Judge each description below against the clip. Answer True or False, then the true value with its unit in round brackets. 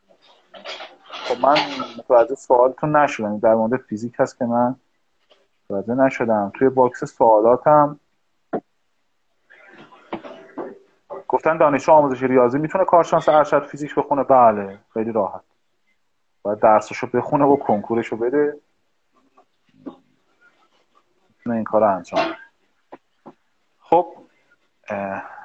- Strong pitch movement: False (4.3 semitones)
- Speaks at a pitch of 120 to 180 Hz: True (135 Hz)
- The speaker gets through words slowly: True (90 wpm)